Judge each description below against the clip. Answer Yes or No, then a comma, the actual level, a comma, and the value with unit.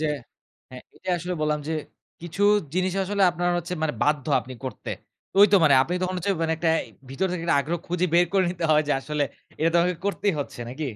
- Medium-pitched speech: Yes, medium, 170 Hz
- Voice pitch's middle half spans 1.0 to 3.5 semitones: Yes, average, 3.2 semitones